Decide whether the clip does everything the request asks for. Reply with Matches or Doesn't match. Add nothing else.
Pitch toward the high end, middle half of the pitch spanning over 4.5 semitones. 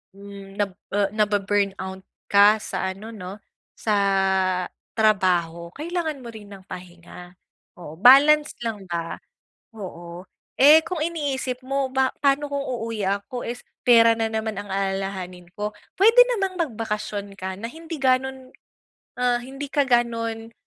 Matches